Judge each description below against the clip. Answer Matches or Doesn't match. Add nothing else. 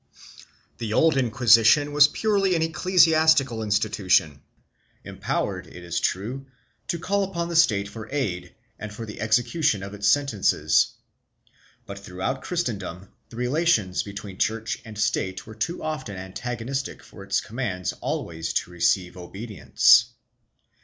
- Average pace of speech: Doesn't match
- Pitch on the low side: Matches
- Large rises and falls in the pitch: Matches